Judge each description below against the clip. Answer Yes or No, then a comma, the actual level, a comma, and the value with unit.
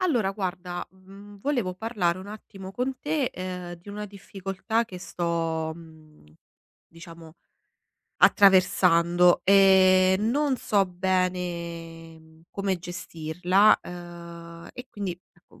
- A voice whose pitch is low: No, medium, 185 Hz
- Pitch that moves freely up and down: No, average, 2.7 semitones